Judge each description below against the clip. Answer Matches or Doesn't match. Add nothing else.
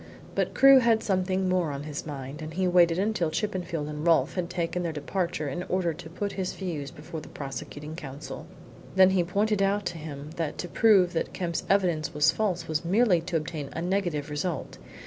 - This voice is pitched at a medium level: Matches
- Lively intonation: Doesn't match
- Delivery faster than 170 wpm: Matches